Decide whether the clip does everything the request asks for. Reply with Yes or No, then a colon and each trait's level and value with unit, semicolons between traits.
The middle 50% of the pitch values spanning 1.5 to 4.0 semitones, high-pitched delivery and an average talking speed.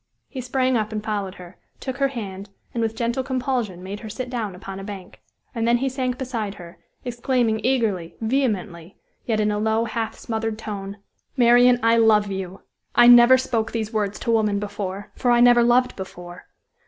Yes: average, 3.3 semitones; high, 225 Hz; average, 190 wpm